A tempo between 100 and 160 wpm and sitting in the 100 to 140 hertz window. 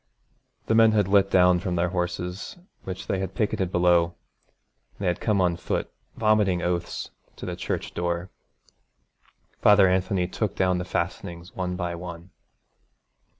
No: average, 150 wpm; very low, 90 Hz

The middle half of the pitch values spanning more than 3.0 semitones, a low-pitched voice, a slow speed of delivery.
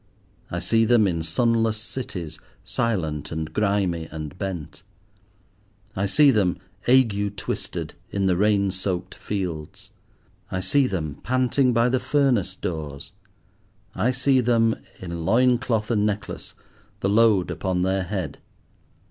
Yes: average, 4.7 semitones; low, 100 Hz; slow, 130 wpm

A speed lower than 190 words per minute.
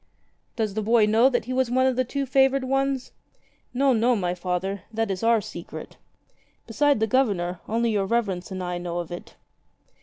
No: average, 195 wpm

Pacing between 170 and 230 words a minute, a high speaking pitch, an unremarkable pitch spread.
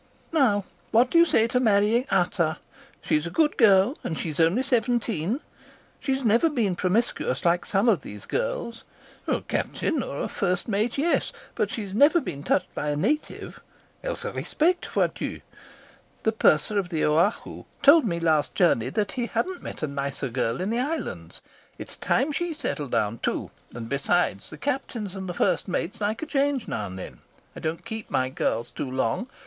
No: average, 175 wpm; high, 205 Hz; wide, 8.4 semitones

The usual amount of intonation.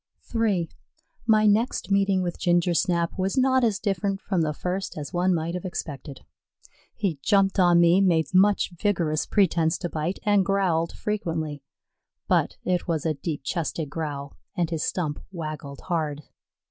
Yes: average, 3.6 semitones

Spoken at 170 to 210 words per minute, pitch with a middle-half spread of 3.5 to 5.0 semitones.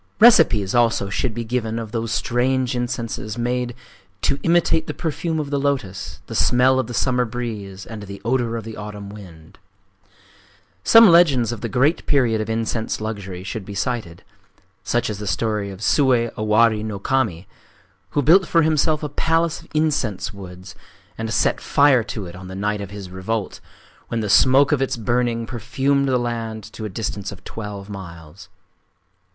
Yes: average, 175 wpm; average, 4.4 semitones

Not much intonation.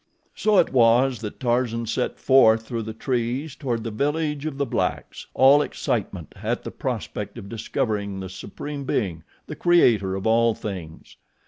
No: average, 4.3 semitones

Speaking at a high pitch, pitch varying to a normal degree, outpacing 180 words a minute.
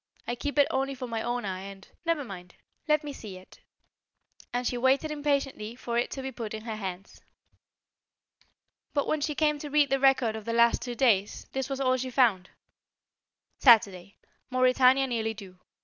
Yes: high, 245 Hz; average, 4.0 semitones; average, 190 wpm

